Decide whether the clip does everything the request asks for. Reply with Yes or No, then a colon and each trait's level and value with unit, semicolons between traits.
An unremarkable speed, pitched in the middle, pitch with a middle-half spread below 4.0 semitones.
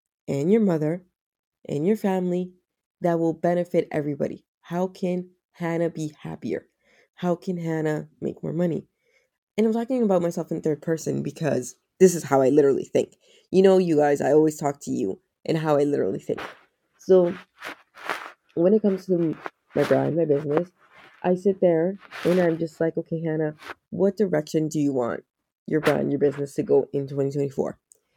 Yes: average, 175 wpm; medium, 165 Hz; average, 3.5 semitones